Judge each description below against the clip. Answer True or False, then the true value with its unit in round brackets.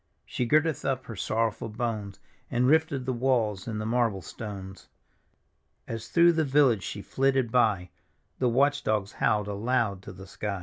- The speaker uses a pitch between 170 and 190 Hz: False (115 Hz)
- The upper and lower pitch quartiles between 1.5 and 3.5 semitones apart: False (4.1 semitones)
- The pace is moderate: True (165 wpm)